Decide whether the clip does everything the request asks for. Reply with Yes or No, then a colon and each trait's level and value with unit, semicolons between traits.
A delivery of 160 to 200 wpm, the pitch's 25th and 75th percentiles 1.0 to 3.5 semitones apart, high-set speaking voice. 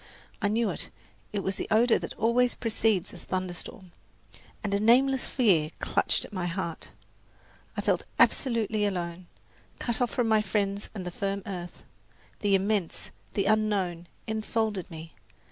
No: average, 150 wpm; average, 3.2 semitones; high, 205 Hz